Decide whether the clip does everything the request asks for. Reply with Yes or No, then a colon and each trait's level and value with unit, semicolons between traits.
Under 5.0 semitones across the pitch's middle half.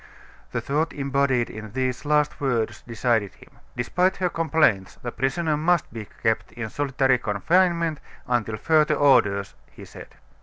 No: wide, 5.4 semitones